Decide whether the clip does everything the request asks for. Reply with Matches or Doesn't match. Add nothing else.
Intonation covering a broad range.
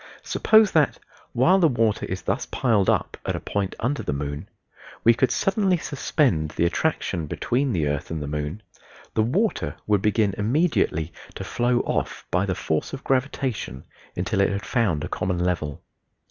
Matches